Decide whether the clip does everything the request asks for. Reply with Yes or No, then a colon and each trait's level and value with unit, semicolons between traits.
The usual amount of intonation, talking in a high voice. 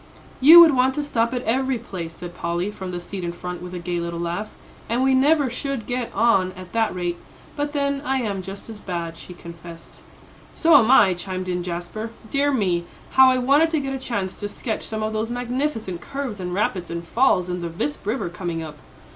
No: wide, 6.7 semitones; high, 205 Hz